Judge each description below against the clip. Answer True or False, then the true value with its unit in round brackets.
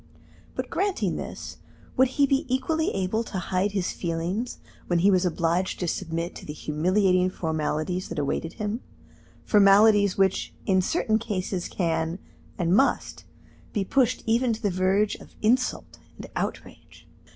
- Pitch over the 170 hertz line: True (190 Hz)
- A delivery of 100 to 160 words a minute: True (150 wpm)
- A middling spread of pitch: True (4.0 semitones)